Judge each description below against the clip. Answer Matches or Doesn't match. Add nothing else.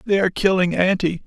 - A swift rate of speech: Doesn't match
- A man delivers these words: Matches